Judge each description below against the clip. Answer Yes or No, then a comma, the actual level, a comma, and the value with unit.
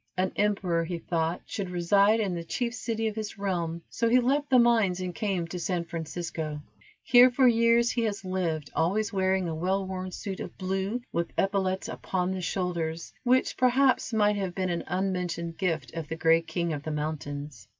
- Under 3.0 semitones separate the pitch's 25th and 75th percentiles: No, average, 3.9 semitones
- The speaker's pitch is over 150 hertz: Yes, medium, 185 Hz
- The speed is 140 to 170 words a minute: No, average, 190 wpm